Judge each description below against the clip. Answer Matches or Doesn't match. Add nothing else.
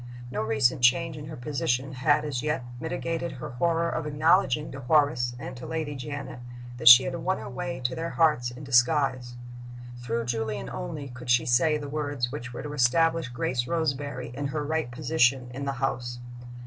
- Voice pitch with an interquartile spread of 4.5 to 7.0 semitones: Doesn't match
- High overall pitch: Doesn't match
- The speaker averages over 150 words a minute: Matches